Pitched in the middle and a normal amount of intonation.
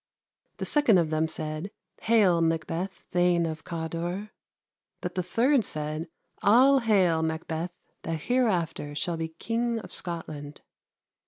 Yes: medium, 170 Hz; average, 4.7 semitones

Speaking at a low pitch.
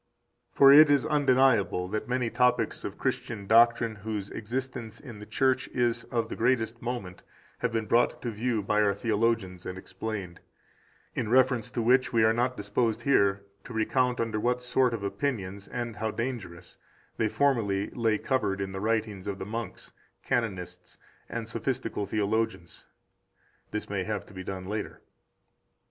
Yes: low, 115 Hz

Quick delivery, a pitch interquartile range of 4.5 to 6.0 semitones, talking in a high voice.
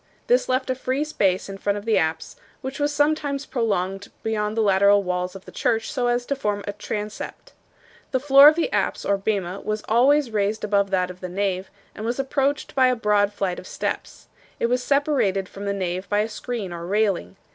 Yes: fast, 210 wpm; average, 4.8 semitones; high, 210 Hz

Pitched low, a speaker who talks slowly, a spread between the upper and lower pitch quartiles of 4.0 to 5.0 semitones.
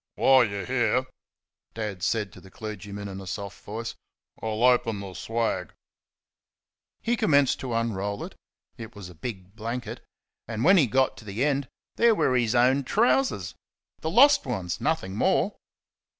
No: low, 115 Hz; average, 165 wpm; average, 4.4 semitones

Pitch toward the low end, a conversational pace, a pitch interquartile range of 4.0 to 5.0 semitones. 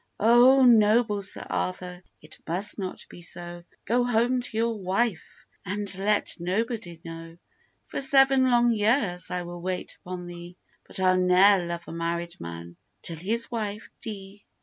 No: high, 195 Hz; average, 155 wpm; average, 4.7 semitones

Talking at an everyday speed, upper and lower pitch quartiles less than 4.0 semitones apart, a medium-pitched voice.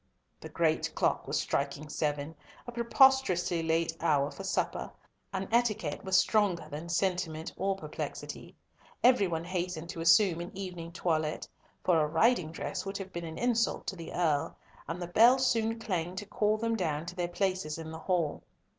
Yes: average, 175 wpm; average, 3.6 semitones; medium, 180 Hz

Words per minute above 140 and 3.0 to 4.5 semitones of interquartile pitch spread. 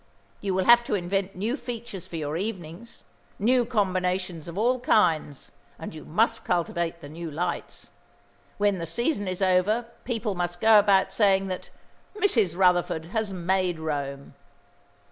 Yes: average, 150 wpm; average, 3.9 semitones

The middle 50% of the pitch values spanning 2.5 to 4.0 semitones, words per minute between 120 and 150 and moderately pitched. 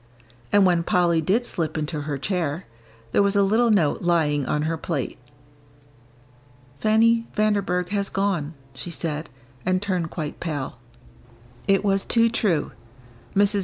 No: average, 4.4 semitones; average, 140 wpm; medium, 180 Hz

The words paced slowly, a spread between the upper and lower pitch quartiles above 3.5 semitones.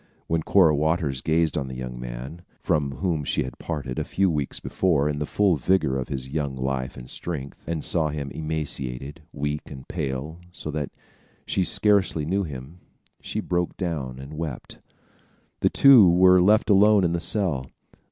No: average, 175 wpm; average, 4.4 semitones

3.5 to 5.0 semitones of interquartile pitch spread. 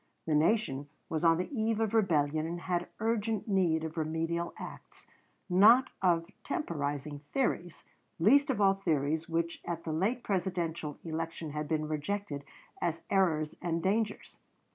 Yes: average, 4.3 semitones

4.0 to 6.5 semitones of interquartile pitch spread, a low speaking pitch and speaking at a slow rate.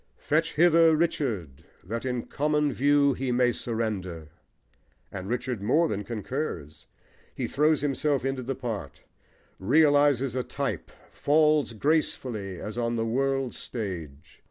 Yes: average, 5.3 semitones; low, 125 Hz; slow, 130 wpm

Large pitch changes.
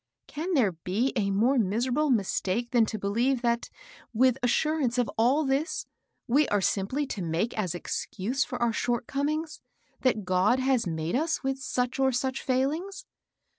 No: average, 4.2 semitones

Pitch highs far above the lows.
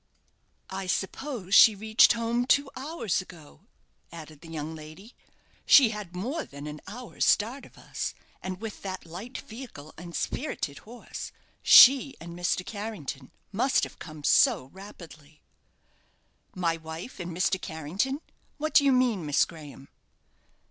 Yes: wide, 6.9 semitones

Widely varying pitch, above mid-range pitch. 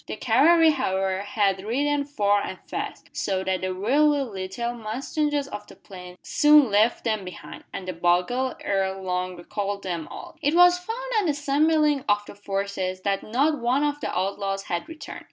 Yes: wide, 7.1 semitones; high, 210 Hz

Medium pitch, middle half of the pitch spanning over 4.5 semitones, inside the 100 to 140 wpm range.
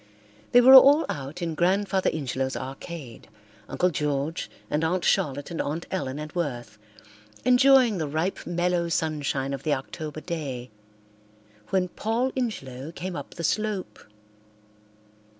Yes: medium, 165 Hz; average, 5.0 semitones; slow, 135 wpm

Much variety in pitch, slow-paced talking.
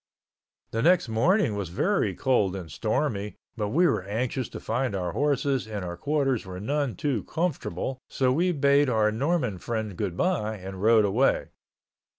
No: wide, 5.7 semitones; average, 160 wpm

